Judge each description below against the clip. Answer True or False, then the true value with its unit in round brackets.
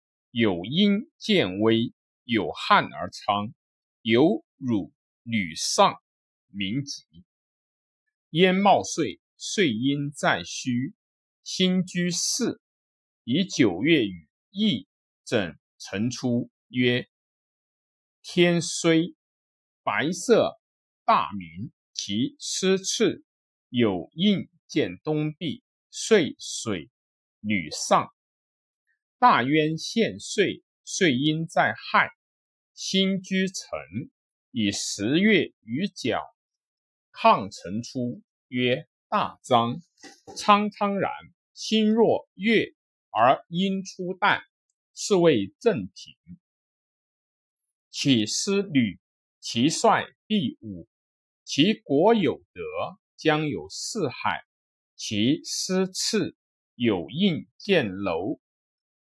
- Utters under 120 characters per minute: True (110 characters per minute)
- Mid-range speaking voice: True (165 Hz)